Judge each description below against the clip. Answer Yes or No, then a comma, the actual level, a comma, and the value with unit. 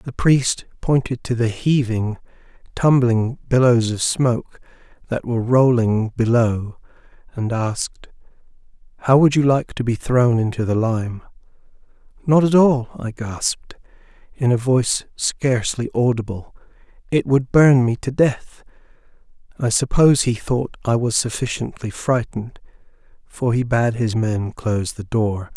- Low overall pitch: Yes, low, 120 Hz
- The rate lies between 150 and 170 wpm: No, slow, 135 wpm